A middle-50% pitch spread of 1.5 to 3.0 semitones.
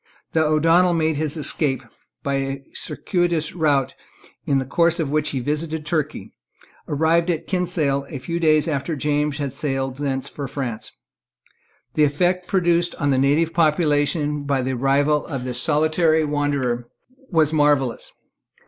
Yes: average, 2.7 semitones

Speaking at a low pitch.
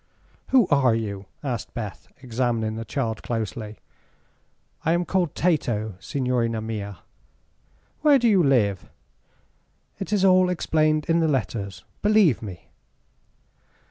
Yes: low, 125 Hz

